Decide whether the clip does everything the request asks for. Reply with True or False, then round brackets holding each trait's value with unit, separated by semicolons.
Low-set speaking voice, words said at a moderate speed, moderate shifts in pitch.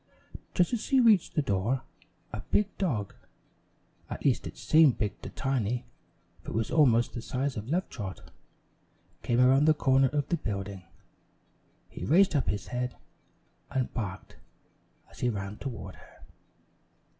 False (130 Hz; 155 wpm; 5.9 semitones)